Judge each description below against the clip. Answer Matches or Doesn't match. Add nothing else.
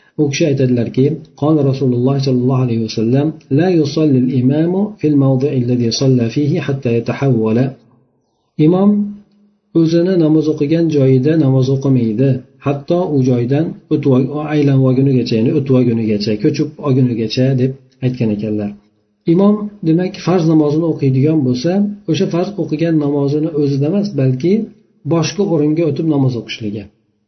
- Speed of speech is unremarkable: Doesn't match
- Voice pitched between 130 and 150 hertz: Matches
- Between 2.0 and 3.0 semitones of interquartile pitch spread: Doesn't match